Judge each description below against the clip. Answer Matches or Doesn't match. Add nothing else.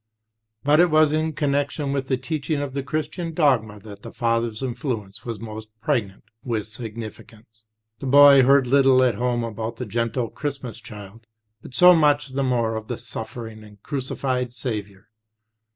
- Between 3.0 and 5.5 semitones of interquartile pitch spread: Matches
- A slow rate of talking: Doesn't match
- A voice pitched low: Matches